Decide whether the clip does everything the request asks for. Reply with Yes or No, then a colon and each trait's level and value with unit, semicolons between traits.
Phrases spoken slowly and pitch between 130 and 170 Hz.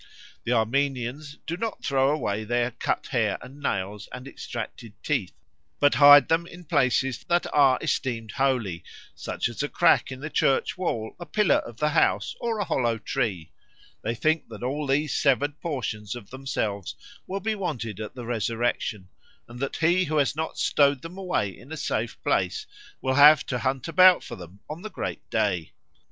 No: average, 180 wpm; low, 135 Hz